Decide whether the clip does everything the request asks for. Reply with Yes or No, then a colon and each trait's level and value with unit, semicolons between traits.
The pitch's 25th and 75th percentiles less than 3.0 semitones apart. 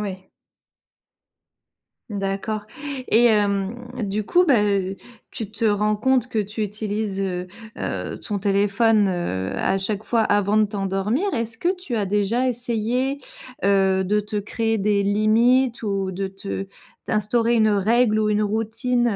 Yes: narrow, 2.6 semitones